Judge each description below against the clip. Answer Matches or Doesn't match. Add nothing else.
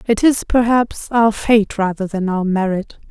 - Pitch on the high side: Matches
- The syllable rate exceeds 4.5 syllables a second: Doesn't match